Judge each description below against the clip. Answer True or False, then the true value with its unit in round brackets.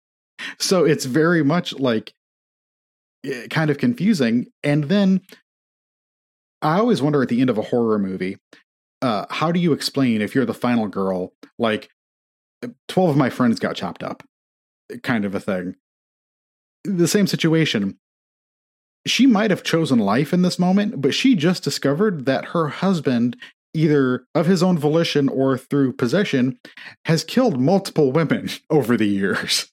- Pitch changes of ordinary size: False (6.6 semitones)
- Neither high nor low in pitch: True (150 Hz)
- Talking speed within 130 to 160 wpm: True (150 wpm)